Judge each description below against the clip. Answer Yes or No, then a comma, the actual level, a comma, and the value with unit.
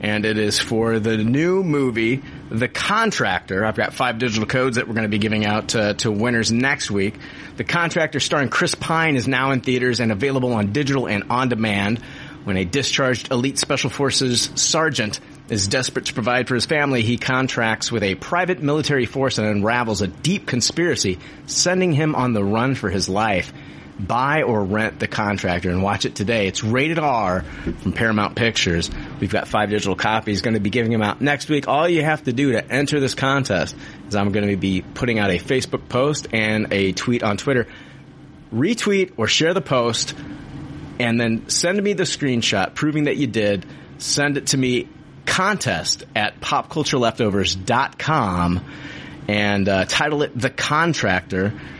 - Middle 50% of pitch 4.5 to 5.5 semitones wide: Yes, average, 5.1 semitones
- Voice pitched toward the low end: Yes, low, 120 Hz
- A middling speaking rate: Yes, average, 180 wpm